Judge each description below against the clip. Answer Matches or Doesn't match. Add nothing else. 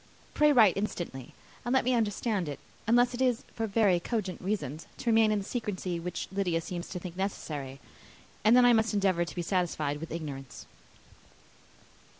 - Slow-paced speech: Doesn't match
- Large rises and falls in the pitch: Doesn't match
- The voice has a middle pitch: Doesn't match